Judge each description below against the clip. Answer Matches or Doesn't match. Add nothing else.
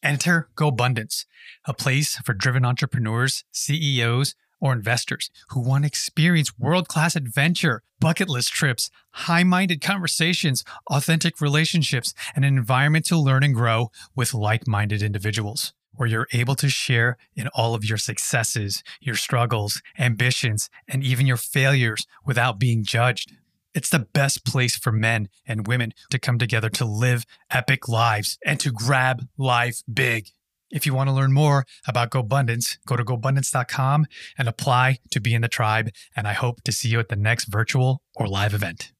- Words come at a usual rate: Matches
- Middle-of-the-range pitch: Doesn't match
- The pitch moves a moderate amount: Matches